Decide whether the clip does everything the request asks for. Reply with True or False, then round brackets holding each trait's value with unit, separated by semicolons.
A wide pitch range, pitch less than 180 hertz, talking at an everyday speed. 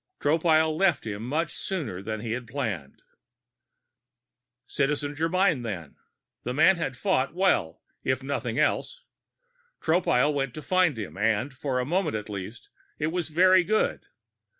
True (6.5 semitones; 140 Hz; 145 wpm)